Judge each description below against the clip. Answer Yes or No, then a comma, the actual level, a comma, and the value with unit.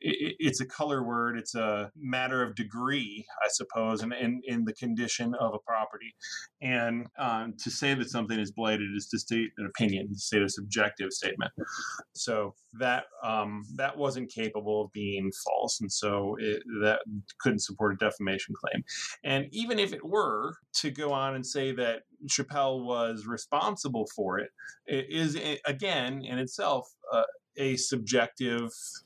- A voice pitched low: Yes, low, 120 Hz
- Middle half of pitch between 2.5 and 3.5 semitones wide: No, average, 4.0 semitones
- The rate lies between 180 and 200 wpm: No, average, 160 wpm